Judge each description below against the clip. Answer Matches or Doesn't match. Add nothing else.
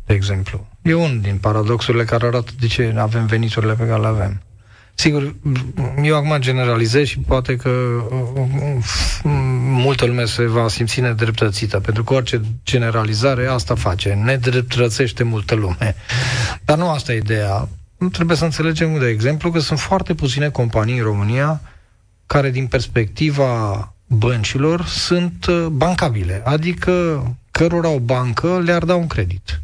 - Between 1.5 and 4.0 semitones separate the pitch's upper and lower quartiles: Doesn't match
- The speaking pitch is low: Matches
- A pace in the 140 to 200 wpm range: Matches